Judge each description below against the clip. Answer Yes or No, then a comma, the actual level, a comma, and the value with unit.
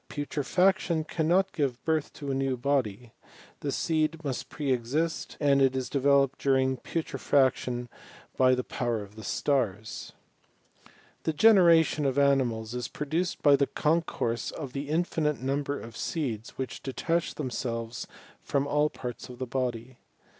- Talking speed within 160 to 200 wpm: No, average, 145 wpm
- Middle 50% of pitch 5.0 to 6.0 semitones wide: No, average, 3.6 semitones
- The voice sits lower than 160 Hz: Yes, medium, 140 Hz